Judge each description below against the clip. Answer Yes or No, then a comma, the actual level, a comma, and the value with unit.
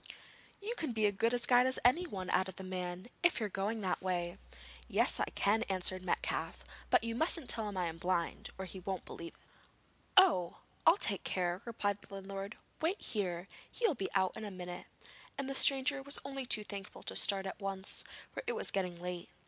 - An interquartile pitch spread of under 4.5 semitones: No, average, 4.9 semitones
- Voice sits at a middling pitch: No, high, 195 Hz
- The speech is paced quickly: Yes, fast, 210 wpm